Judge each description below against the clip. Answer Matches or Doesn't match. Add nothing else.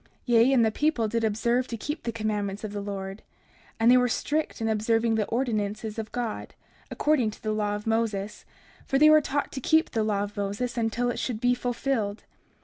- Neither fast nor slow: Doesn't match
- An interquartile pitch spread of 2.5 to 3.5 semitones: Matches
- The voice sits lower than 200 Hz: Doesn't match